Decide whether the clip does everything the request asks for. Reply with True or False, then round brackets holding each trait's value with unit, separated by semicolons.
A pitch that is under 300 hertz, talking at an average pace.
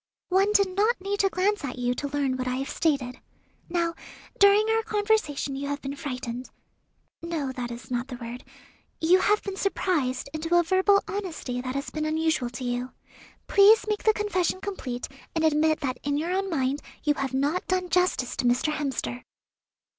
False (310 Hz; 185 wpm)